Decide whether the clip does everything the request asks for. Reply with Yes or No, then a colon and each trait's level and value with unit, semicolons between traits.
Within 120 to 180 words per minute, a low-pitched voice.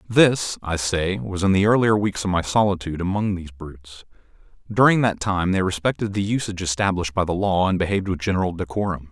No: average, 200 wpm; very low, 95 Hz